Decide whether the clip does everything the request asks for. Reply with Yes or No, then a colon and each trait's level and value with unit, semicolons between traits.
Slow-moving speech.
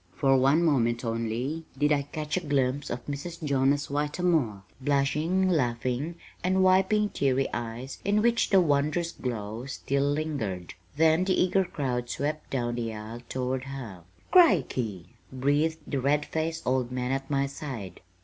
No: average, 150 wpm